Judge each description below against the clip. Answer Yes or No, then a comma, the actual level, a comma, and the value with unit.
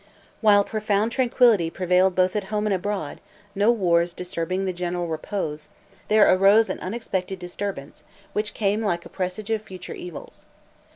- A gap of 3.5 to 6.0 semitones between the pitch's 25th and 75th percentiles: No, average, 3.0 semitones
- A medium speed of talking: Yes, average, 155 wpm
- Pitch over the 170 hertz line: Yes, high, 190 Hz